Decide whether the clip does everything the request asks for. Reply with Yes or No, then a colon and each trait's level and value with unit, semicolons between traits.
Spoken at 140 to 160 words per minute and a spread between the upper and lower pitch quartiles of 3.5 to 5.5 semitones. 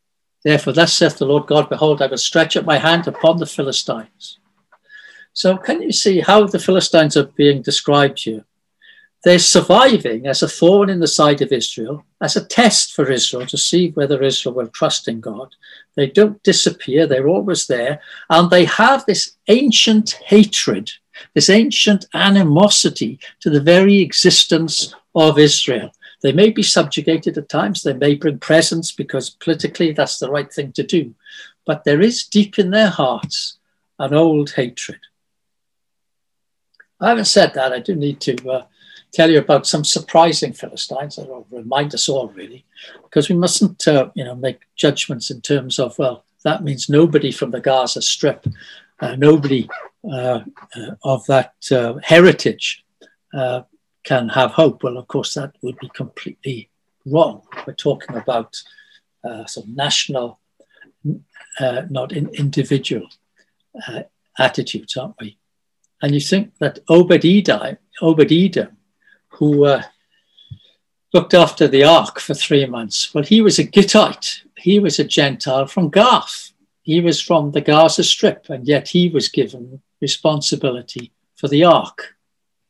Yes: average, 155 wpm; average, 5.0 semitones